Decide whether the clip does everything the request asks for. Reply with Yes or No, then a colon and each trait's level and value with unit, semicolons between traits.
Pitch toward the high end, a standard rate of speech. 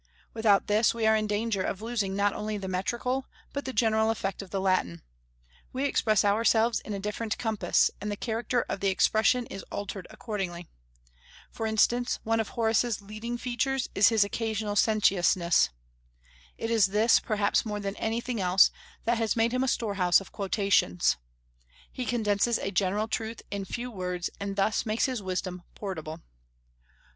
Yes: high, 215 Hz; average, 170 wpm